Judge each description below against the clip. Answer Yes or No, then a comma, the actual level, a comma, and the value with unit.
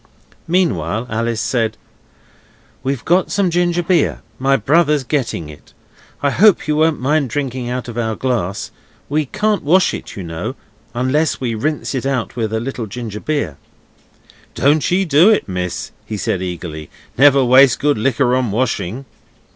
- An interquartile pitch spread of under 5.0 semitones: No, wide, 5.4 semitones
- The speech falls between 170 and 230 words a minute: No, average, 160 wpm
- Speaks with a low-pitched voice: Yes, low, 130 Hz